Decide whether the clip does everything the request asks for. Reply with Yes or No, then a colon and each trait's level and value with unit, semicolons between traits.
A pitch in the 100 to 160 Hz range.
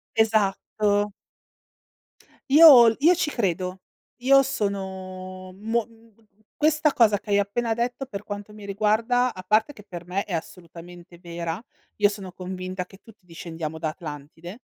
No: high, 200 Hz